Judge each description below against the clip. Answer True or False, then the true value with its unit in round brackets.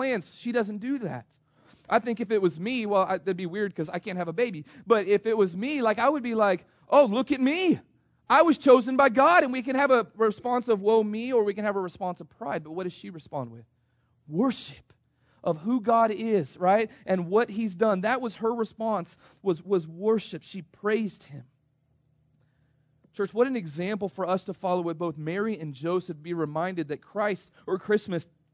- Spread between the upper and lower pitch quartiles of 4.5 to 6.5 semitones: True (5.1 semitones)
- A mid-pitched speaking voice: False (200 Hz)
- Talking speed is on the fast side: True (215 wpm)